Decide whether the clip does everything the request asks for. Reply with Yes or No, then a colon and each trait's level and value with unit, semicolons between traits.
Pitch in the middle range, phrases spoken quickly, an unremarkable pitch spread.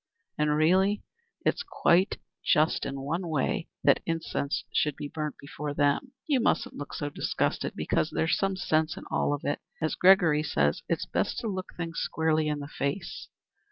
No: medium, 155 Hz; average, 170 wpm; average, 3.6 semitones